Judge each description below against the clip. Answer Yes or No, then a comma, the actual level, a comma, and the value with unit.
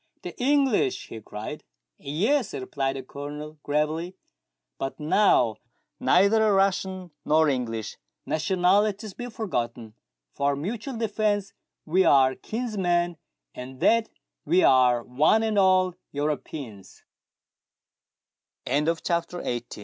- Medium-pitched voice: Yes, medium, 165 Hz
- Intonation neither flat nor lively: No, wide, 7.0 semitones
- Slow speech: Yes, slow, 120 wpm